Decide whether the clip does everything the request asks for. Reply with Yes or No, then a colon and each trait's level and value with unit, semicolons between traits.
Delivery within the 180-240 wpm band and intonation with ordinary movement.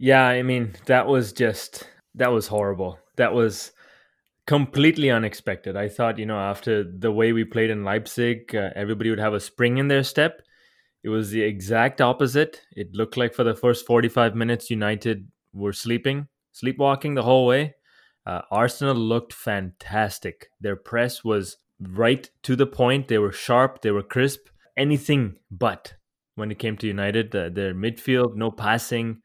No: average, 170 wpm; average, 3.3 semitones